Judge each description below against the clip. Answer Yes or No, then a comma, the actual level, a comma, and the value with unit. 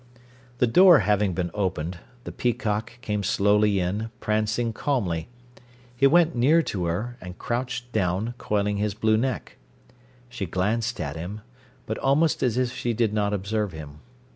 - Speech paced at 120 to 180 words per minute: Yes, average, 155 wpm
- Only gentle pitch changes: No, average, 3.9 semitones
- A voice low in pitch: Yes, low, 105 Hz